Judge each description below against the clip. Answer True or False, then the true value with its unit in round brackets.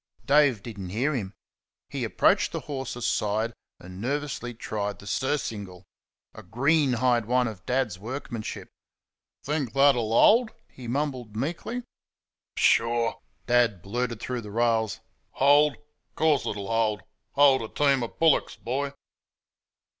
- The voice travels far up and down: False (4.2 semitones)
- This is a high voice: False (120 Hz)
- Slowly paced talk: True (130 wpm)